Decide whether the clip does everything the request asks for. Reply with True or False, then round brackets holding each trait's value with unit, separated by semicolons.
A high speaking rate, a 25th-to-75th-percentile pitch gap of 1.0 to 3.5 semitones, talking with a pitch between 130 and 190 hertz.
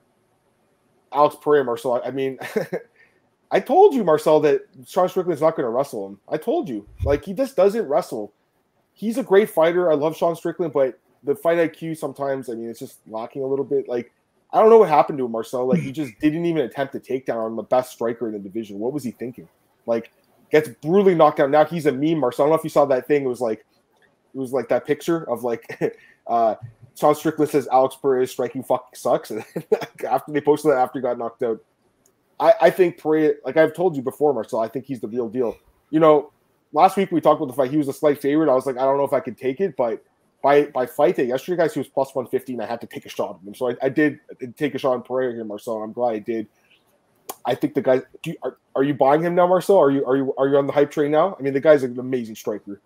False (260 wpm; 3.9 semitones; 140 Hz)